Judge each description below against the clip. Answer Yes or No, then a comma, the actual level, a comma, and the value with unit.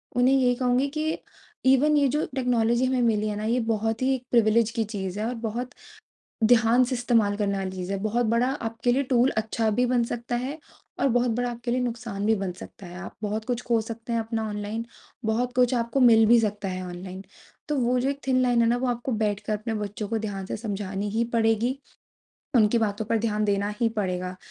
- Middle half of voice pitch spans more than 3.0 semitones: No, average, 2.7 semitones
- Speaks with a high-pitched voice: Yes, high, 230 Hz